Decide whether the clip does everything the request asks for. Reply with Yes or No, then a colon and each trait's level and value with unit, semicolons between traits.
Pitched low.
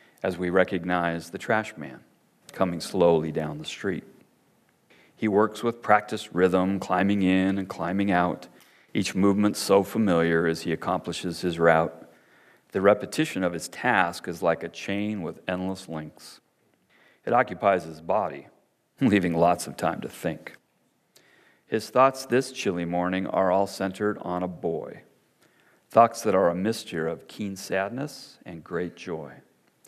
Yes: very low, 95 Hz